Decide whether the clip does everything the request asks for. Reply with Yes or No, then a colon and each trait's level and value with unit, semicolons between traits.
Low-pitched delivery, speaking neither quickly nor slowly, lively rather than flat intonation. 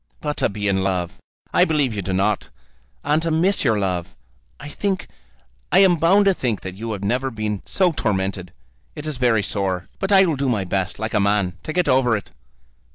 No: low, 115 Hz; fast, 215 wpm; wide, 8.0 semitones